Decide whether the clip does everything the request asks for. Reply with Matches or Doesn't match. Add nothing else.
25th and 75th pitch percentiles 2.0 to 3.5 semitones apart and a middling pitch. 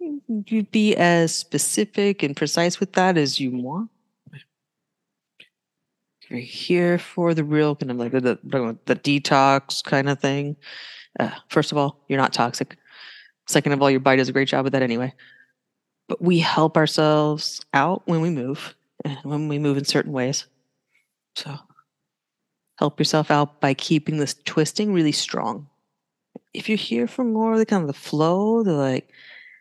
Doesn't match